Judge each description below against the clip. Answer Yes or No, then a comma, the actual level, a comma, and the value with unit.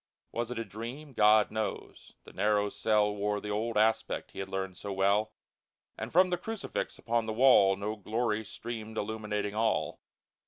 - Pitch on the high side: No, low, 110 Hz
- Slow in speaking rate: No, average, 170 wpm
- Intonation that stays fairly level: Yes, narrow, 1.8 semitones